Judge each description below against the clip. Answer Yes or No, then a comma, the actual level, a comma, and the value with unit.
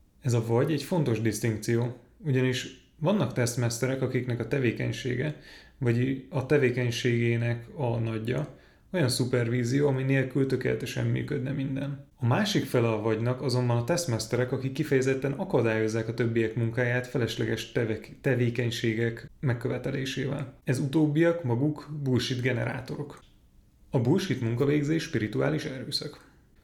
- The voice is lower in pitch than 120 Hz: No, low, 125 Hz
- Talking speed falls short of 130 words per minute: Yes, average, 115 wpm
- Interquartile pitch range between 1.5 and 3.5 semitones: Yes, average, 2.9 semitones